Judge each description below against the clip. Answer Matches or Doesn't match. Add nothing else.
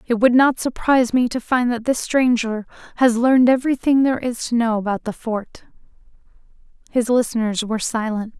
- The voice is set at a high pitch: Matches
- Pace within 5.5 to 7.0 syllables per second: Matches